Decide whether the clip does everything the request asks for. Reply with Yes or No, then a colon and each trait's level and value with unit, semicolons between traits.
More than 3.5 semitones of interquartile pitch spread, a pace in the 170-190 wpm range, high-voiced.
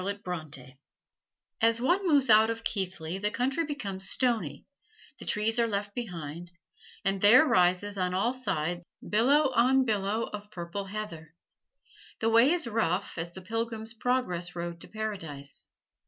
No: average, 4.5 semitones; average, 140 wpm; high, 210 Hz